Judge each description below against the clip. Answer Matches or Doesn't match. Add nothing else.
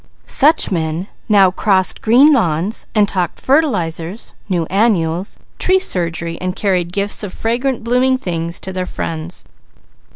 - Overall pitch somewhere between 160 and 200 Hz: Matches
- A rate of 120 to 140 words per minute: Matches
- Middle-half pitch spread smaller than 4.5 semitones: Doesn't match